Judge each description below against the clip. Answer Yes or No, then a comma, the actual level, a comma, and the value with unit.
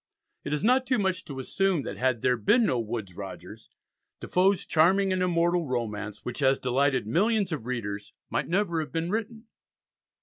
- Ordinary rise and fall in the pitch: No, wide, 7.6 semitones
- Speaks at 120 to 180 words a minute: Yes, average, 175 wpm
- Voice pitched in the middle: Yes, medium, 155 Hz